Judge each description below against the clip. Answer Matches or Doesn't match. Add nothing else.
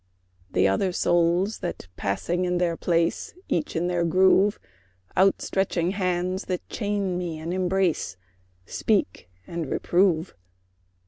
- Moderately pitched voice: Matches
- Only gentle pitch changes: Matches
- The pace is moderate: Doesn't match